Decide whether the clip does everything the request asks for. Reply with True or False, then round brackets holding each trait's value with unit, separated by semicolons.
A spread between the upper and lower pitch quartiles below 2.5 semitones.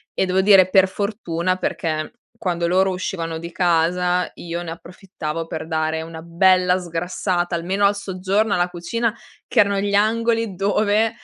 False (2.8 semitones)